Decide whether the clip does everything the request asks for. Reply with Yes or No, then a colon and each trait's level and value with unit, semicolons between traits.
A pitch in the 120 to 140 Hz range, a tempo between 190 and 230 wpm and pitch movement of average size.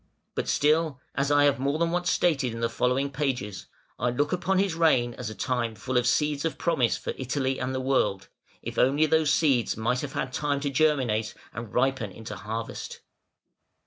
Yes: low, 135 Hz; average, 195 wpm; average, 3.7 semitones